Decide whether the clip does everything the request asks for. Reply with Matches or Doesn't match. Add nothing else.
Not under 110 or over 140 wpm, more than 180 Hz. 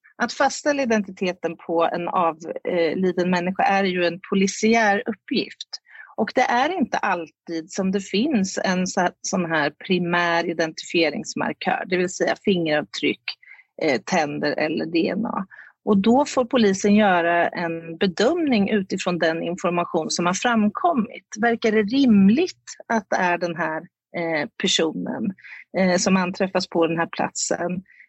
Matches